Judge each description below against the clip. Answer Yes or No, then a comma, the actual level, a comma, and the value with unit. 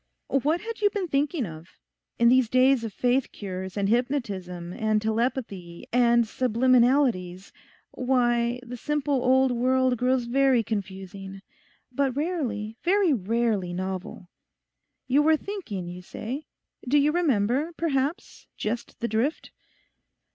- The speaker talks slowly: Yes, slow, 125 wpm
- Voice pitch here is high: Yes, high, 245 Hz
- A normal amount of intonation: Yes, average, 4.7 semitones